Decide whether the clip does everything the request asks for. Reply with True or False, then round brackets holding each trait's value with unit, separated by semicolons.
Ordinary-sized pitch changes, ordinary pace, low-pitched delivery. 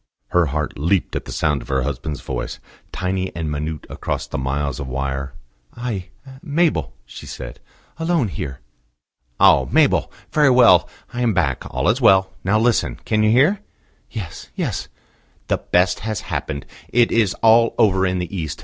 False (7.6 semitones; 165 wpm; 90 Hz)